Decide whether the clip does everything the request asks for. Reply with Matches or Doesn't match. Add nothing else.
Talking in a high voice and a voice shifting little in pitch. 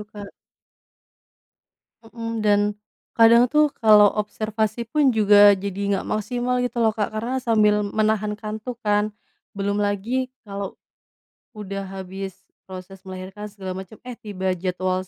Matches